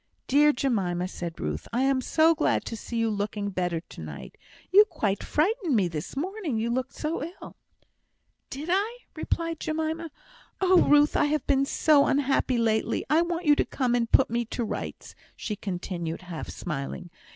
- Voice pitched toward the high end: Yes, very high, 260 Hz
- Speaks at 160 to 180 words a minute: Yes, average, 175 wpm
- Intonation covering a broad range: Yes, wide, 7.6 semitones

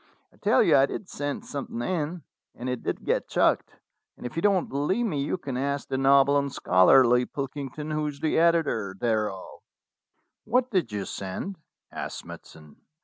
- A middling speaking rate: Yes, average, 180 wpm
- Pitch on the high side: No, medium, 140 Hz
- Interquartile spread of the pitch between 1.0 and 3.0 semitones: No, wide, 5.4 semitones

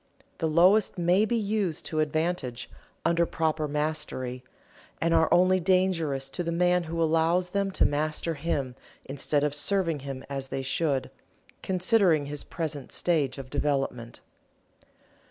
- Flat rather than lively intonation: No, average, 3.8 semitones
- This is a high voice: No, medium, 160 Hz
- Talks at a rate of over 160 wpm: No, average, 140 wpm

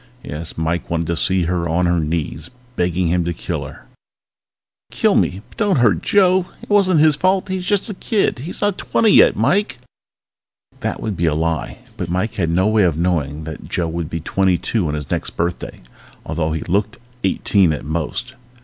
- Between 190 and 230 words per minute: Yes, average, 195 wpm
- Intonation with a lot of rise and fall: Yes, wide, 7.2 semitones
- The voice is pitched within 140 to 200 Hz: No, very low, 90 Hz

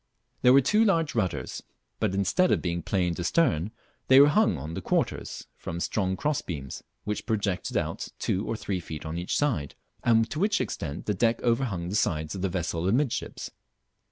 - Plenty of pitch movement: Yes, wide, 7.1 semitones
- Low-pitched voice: Yes, low, 100 Hz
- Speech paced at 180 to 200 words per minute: Yes, average, 185 wpm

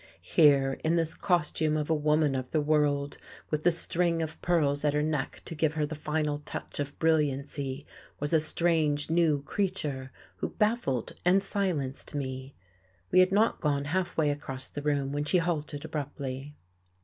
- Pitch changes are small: Yes, narrow, 2.3 semitones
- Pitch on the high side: No, medium, 150 Hz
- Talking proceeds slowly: No, average, 170 wpm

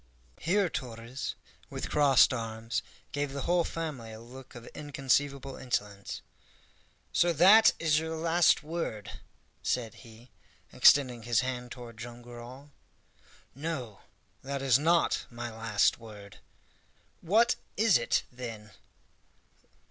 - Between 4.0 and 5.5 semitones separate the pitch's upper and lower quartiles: Yes, average, 4.7 semitones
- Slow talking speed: Yes, slow, 120 wpm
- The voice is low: Yes, low, 130 Hz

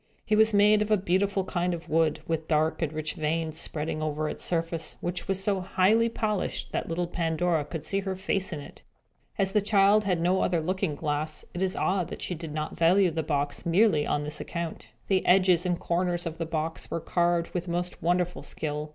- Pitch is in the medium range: Yes, medium, 175 Hz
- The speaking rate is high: Yes, fast, 210 wpm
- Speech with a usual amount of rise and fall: Yes, average, 3.0 semitones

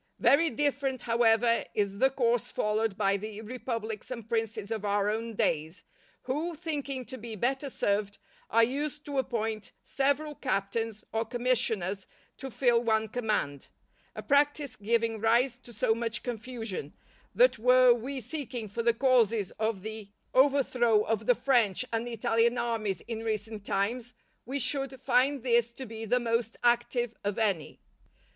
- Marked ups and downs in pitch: No, average, 2.8 semitones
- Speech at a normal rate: Yes, average, 155 wpm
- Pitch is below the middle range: No, high, 230 Hz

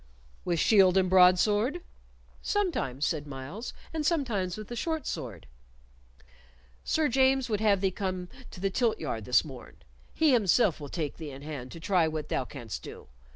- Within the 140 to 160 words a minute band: No, average, 170 wpm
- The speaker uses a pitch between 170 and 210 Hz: Yes, medium, 185 Hz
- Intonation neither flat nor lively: No, wide, 7.9 semitones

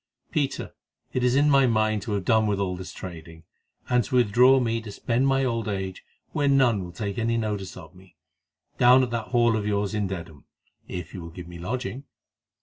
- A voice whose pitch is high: No, low, 110 Hz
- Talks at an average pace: No, fast, 210 wpm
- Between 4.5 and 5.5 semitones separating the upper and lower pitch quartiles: Yes, average, 4.8 semitones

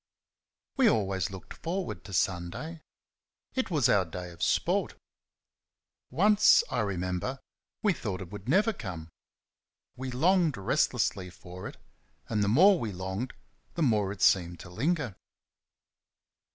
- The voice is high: No, low, 105 Hz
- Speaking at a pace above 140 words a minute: No, slow, 135 wpm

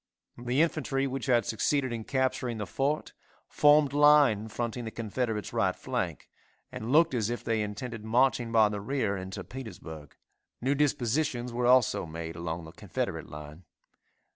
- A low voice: Yes, low, 120 Hz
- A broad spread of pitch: No, average, 4.4 semitones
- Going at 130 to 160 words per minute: Yes, average, 155 wpm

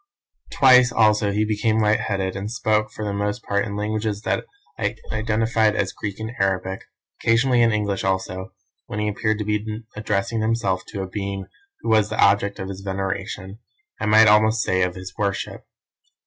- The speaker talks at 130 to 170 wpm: No, average, 180 wpm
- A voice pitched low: Yes, low, 105 Hz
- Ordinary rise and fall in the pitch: No, narrow, 1.9 semitones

